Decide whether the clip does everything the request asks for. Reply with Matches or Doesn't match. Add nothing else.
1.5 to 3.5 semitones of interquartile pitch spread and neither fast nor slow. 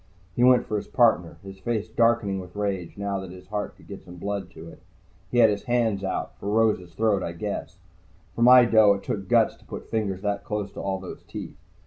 Doesn't match